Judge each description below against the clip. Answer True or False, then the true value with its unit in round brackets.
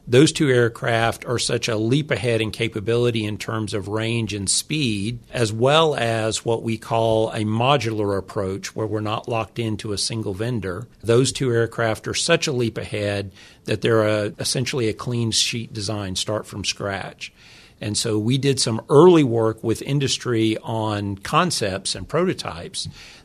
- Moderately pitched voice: False (115 Hz)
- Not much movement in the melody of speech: True (2.0 semitones)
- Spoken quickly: False (170 wpm)